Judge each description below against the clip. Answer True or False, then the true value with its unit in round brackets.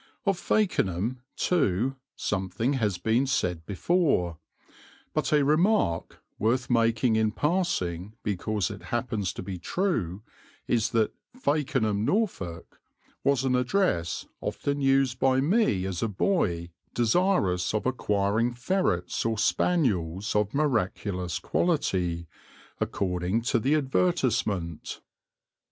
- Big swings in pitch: True (7.1 semitones)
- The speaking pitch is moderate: False (115 Hz)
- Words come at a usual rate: False (110 wpm)